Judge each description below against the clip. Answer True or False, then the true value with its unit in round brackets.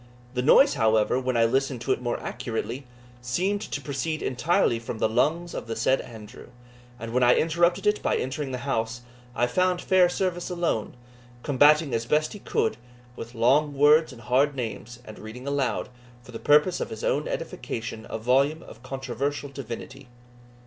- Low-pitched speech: True (130 Hz)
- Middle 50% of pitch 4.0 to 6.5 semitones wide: True (4.6 semitones)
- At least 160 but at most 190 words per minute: True (175 wpm)